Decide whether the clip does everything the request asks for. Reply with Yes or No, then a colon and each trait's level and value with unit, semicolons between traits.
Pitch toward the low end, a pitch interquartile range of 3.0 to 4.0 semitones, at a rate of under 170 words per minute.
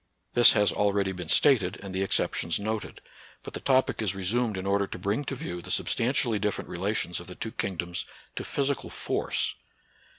No: low, 100 Hz; average, 3.6 semitones; average, 185 wpm